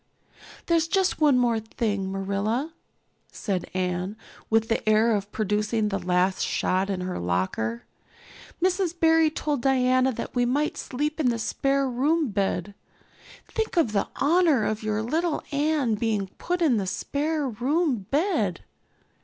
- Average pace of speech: Yes, average, 145 wpm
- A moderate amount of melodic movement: No, wide, 7.0 semitones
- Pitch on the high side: Yes, high, 235 Hz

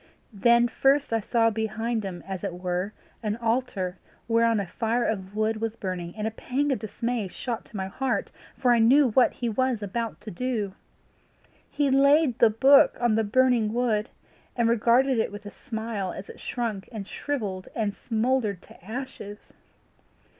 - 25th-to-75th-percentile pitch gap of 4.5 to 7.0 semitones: No, average, 3.1 semitones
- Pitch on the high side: Yes, high, 225 Hz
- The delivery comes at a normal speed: Yes, average, 175 wpm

